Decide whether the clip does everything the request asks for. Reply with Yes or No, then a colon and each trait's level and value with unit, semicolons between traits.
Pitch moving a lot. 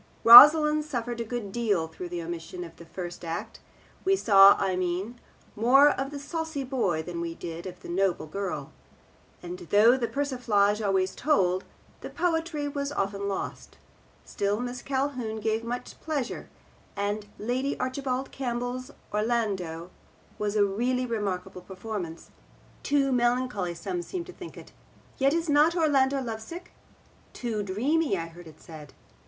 Yes: wide, 6.4 semitones